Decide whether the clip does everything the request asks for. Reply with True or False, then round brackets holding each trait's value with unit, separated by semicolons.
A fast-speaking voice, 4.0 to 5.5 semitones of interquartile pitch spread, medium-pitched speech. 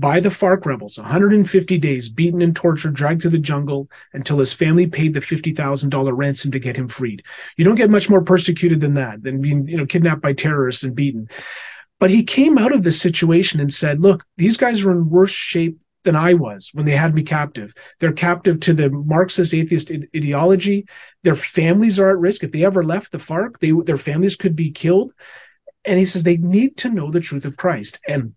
True (215 wpm; 4.4 semitones; 170 Hz)